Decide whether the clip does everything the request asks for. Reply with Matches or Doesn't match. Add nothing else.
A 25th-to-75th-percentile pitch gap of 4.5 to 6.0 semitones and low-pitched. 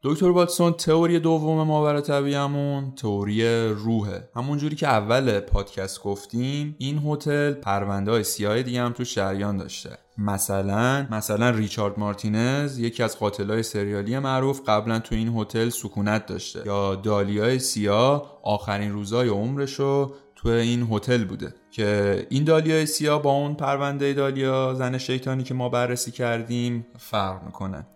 Matches